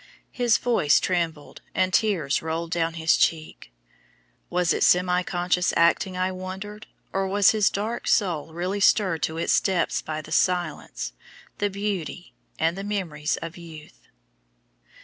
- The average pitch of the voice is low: No, medium, 180 Hz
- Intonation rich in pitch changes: No, average, 3.0 semitones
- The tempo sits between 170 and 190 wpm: No, average, 145 wpm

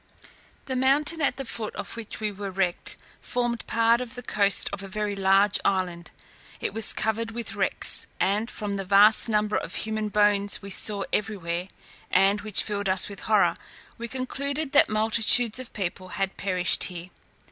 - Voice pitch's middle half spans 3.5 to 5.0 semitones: No, average, 2.8 semitones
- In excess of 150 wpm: Yes, average, 175 wpm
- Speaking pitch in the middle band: No, high, 210 Hz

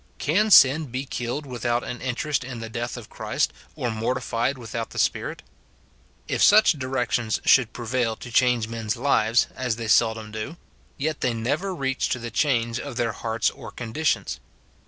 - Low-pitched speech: Yes, low, 120 Hz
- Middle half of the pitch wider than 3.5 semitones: No, average, 2.7 semitones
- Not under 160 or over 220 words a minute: Yes, average, 170 wpm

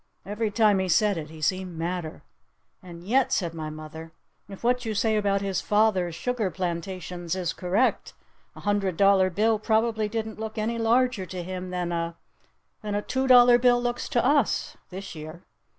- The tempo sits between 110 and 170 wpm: No, average, 180 wpm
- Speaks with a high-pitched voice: Yes, high, 195 Hz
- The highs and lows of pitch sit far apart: No, average, 4.1 semitones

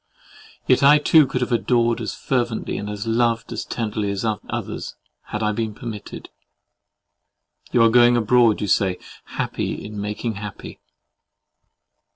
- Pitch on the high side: No, low, 115 Hz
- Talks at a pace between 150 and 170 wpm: No, average, 140 wpm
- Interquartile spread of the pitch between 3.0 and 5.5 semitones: No, narrow, 2.5 semitones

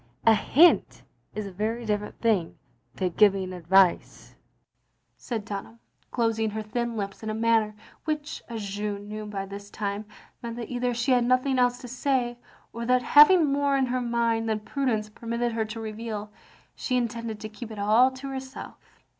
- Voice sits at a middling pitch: No, high, 225 Hz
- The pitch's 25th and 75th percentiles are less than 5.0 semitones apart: Yes, average, 2.8 semitones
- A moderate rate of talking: Yes, average, 180 wpm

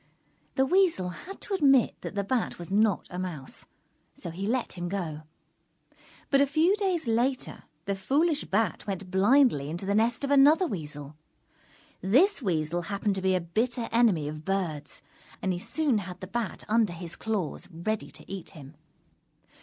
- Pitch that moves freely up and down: Yes, wide, 6.8 semitones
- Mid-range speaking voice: No, high, 200 Hz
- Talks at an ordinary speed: Yes, average, 170 wpm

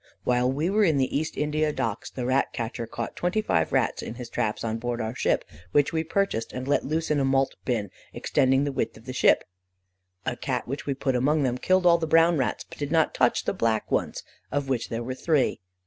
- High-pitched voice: No, low, 135 Hz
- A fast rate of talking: Yes, fast, 235 wpm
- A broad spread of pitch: No, average, 4.2 semitones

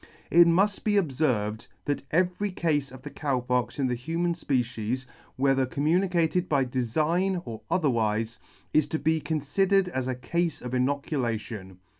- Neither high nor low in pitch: Yes, medium, 145 Hz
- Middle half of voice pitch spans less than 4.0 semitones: No, average, 5.2 semitones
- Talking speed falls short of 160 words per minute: Yes, average, 150 wpm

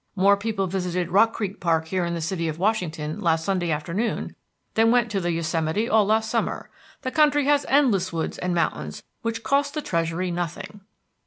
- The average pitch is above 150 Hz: Yes, medium, 185 Hz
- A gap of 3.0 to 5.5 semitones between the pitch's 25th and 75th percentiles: Yes, average, 4.8 semitones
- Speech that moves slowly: No, average, 185 wpm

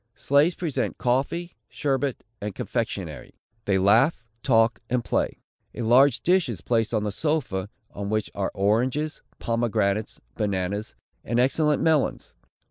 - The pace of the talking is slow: Yes, slow, 130 wpm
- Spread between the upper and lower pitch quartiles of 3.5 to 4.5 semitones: No, wide, 5.4 semitones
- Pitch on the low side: Yes, low, 120 Hz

